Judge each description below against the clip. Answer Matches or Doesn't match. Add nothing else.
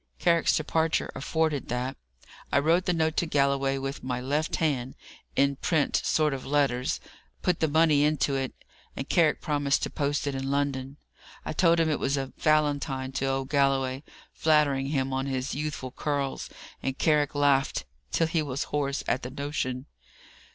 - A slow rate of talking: Doesn't match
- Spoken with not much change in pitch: Matches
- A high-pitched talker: Doesn't match